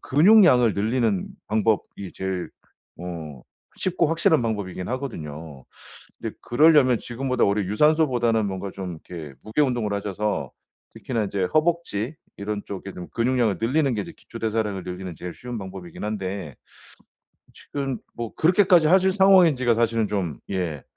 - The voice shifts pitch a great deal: Yes, wide, 6.0 semitones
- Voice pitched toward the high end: No, low, 110 Hz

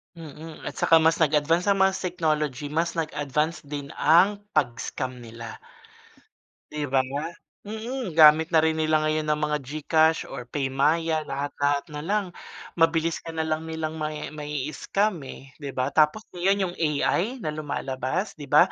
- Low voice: No, medium, 155 Hz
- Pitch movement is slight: Yes, narrow, 2.3 semitones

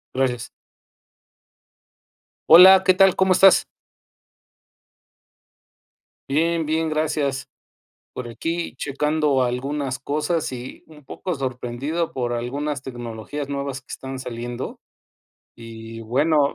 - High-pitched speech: No, medium, 140 Hz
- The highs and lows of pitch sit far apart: No, average, 4.0 semitones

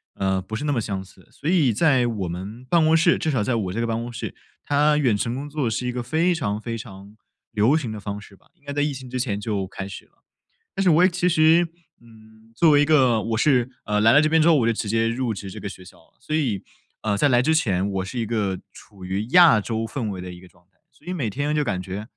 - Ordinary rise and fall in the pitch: No, wide, 6.1 semitones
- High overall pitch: No, low, 115 Hz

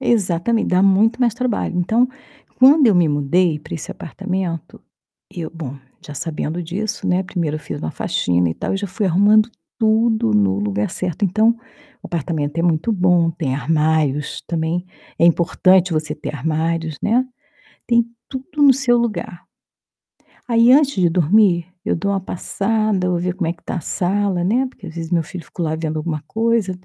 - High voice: No, medium, 180 Hz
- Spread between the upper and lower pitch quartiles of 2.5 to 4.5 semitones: No, average, 5.2 semitones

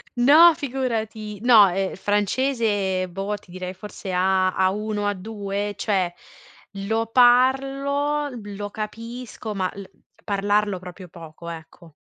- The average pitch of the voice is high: Yes, high, 205 Hz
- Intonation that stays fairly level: No, average, 4.0 semitones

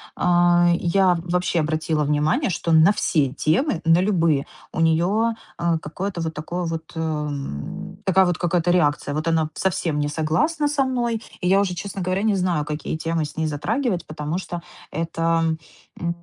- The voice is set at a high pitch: No, medium, 170 Hz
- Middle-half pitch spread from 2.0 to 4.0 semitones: Yes, average, 2.9 semitones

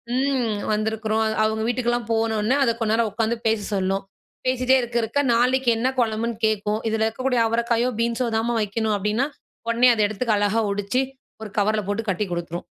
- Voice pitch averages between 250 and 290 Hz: No, high, 225 Hz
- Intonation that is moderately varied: No, narrow, 1.9 semitones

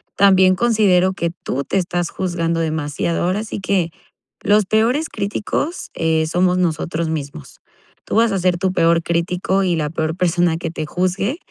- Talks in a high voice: No, medium, 180 Hz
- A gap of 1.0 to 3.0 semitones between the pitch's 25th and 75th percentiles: Yes, average, 2.7 semitones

